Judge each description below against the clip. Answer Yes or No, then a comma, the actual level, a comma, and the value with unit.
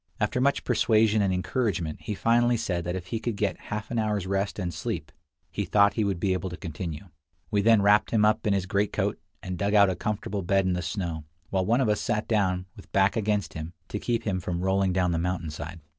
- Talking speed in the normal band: No, fast, 235 wpm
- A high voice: No, low, 100 Hz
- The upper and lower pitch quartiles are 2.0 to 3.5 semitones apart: Yes, average, 2.9 semitones